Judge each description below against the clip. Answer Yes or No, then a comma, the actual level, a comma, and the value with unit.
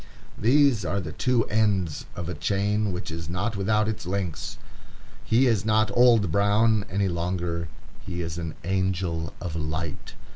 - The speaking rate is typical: Yes, average, 155 wpm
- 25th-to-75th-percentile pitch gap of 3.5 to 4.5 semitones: Yes, average, 4.1 semitones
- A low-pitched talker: Yes, very low, 95 Hz